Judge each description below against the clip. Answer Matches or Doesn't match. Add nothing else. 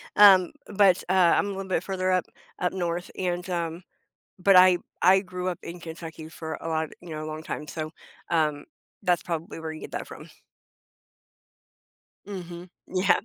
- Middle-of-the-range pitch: Matches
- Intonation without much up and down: Matches